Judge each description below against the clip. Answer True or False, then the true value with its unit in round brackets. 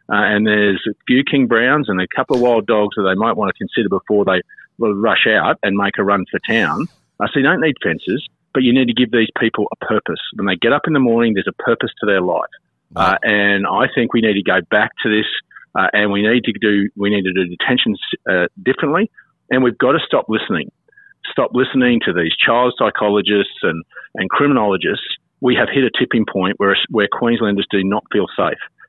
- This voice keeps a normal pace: False (220 wpm)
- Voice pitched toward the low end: True (110 Hz)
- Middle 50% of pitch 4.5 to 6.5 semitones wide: False (3.6 semitones)